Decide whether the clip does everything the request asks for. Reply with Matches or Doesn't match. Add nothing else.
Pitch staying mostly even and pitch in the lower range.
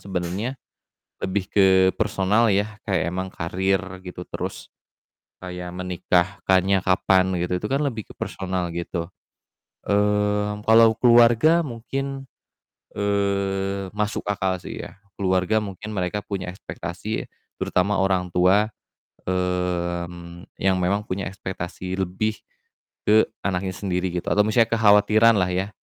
Matches